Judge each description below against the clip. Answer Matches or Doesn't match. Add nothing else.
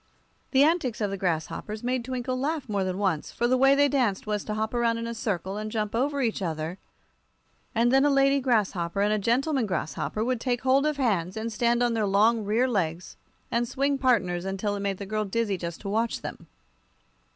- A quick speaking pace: Matches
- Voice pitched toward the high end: Matches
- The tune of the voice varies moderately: Matches